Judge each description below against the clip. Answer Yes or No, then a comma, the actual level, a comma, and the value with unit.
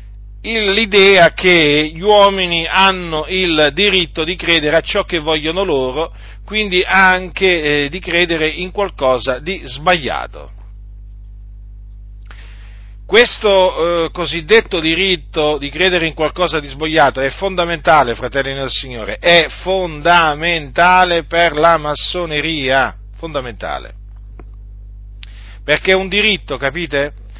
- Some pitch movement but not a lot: No, wide, 5.9 semitones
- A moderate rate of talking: No, slow, 105 wpm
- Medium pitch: Yes, medium, 160 Hz